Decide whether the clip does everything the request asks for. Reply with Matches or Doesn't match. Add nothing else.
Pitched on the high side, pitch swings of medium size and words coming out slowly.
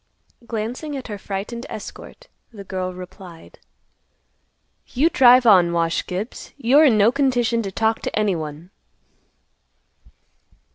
Matches